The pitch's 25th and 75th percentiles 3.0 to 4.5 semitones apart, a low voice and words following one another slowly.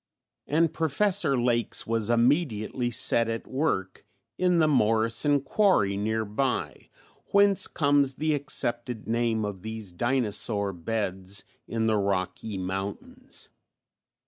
No: wide, 5.5 semitones; low, 115 Hz; slow, 115 wpm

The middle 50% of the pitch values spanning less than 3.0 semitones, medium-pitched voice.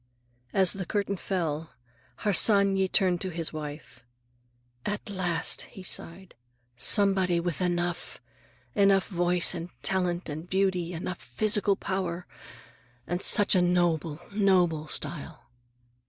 Yes: narrow, 2.4 semitones; medium, 180 Hz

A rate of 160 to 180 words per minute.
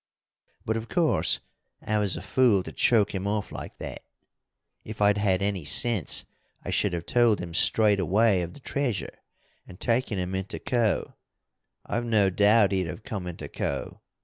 Yes: average, 175 wpm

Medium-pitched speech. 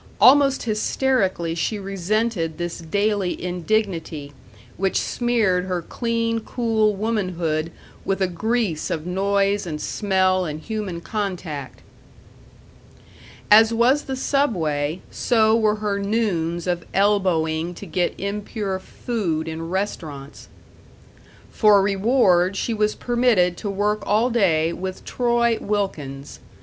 No: high, 195 Hz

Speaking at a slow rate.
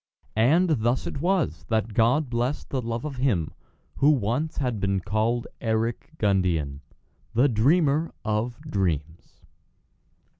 Yes: slow, 125 wpm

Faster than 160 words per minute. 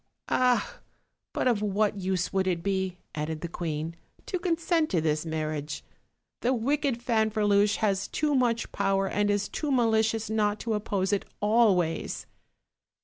No: average, 145 wpm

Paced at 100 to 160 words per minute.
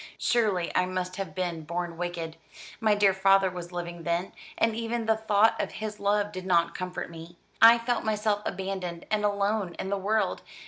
No: average, 185 wpm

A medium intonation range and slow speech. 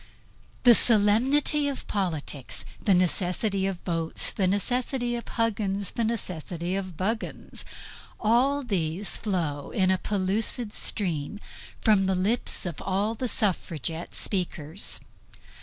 Yes: average, 4.1 semitones; slow, 120 wpm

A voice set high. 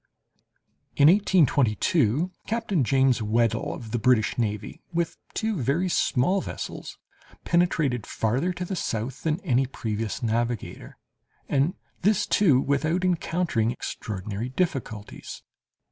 No: low, 135 Hz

